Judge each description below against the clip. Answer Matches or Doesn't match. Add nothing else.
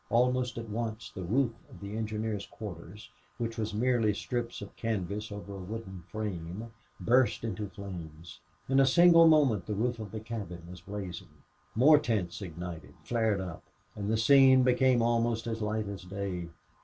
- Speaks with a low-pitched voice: Matches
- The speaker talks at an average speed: Matches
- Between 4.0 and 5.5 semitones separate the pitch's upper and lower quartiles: Doesn't match